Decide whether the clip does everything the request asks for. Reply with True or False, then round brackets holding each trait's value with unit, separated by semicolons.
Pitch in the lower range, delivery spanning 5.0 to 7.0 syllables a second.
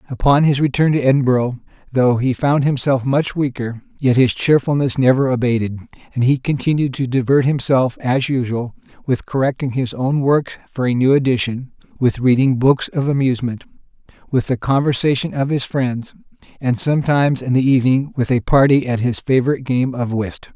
True (130 Hz; 5.4 syllables/s)